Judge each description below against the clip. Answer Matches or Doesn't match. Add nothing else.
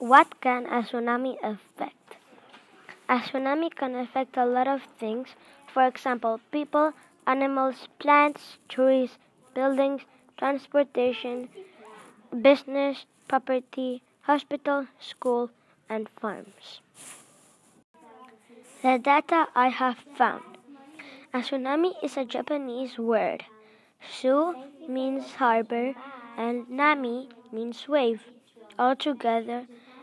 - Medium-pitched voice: Doesn't match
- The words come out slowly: Matches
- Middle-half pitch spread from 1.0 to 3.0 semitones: Matches